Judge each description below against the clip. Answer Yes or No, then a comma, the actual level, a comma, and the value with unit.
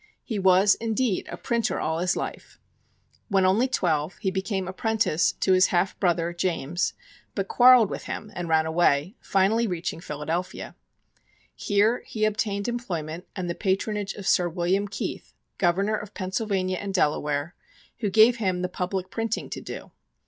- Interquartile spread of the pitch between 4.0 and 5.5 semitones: No, average, 3.2 semitones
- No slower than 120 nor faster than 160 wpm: Yes, average, 155 wpm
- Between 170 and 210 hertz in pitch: Yes, high, 190 Hz